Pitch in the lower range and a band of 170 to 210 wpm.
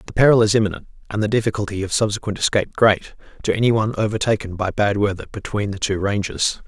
Yes: low, 105 Hz; average, 200 wpm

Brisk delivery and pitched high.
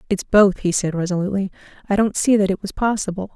Yes: fast, 215 wpm; high, 195 Hz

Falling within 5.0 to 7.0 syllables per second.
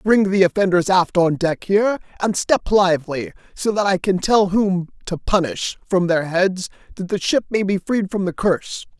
No: 4.8 syllables/s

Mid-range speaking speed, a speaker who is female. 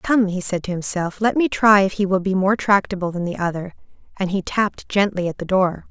No: fast, 245 wpm; female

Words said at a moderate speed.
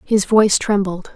Yes: average, 155 wpm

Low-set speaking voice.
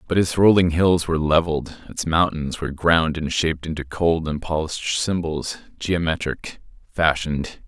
Yes: very low, 80 Hz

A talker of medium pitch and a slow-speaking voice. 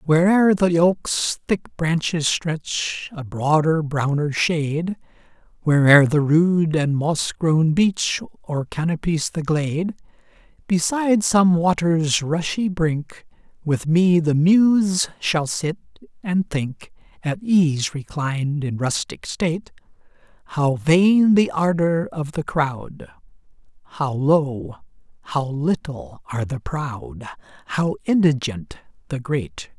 Yes: medium, 160 Hz; slow, 115 wpm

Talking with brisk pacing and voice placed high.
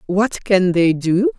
No: average, 175 wpm; high, 200 Hz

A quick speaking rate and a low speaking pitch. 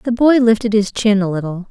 No: fast, 245 wpm; high, 215 Hz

